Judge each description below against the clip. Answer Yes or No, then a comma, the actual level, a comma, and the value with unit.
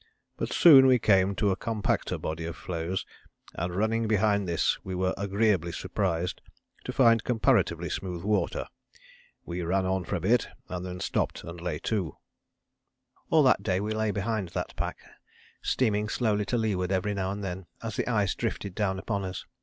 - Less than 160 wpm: No, average, 175 wpm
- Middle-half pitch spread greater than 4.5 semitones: No, average, 3.1 semitones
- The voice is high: No, low, 100 Hz